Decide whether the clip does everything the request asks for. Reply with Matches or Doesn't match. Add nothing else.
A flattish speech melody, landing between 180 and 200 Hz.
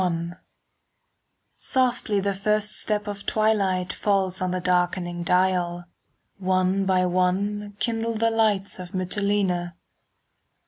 Matches